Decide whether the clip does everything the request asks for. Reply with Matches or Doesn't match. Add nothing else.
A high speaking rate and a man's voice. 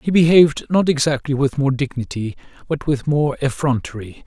Doesn't match